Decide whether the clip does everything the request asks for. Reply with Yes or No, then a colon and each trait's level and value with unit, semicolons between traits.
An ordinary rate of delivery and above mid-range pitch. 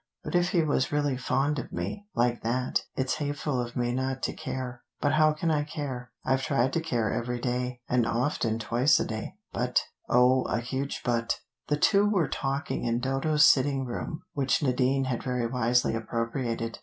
No: average, 185 wpm; low, 130 Hz